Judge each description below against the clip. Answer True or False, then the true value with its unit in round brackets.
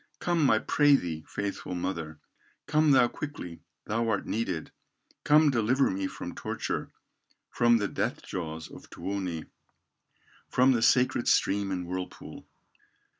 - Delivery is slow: True (130 wpm)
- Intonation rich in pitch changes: True (6.1 semitones)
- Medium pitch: False (105 Hz)